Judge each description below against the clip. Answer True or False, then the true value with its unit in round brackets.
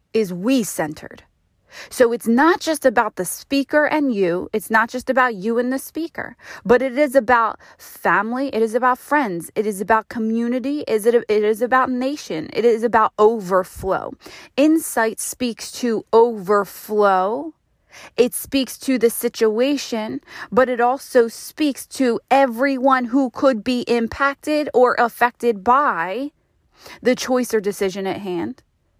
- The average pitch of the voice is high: True (240 Hz)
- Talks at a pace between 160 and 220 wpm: False (145 wpm)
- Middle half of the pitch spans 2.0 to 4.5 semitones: True (3.4 semitones)